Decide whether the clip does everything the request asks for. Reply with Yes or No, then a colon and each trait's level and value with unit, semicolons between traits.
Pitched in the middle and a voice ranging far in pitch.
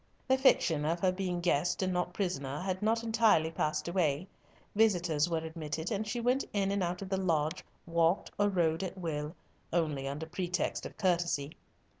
No: medium, 175 Hz; average, 3.4 semitones